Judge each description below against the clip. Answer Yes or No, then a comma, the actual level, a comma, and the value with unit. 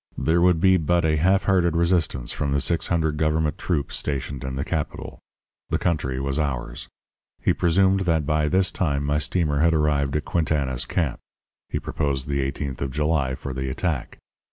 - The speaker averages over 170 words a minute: Yes, average, 180 wpm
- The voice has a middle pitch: No, very low, 75 Hz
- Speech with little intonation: No, average, 3.5 semitones